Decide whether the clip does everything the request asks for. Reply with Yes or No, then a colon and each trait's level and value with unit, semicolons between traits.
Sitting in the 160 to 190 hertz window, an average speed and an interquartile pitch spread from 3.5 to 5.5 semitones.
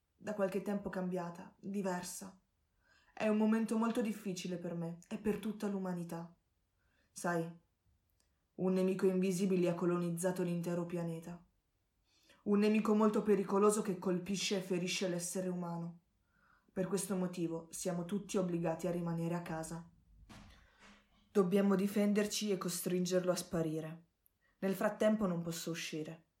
No: medium, 185 Hz; average, 125 wpm; average, 2.7 semitones